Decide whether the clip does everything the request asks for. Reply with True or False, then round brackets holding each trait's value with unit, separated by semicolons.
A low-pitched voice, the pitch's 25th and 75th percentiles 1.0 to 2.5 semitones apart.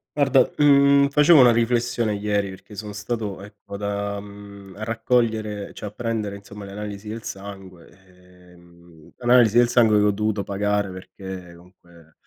False (105 Hz; 2.9 semitones)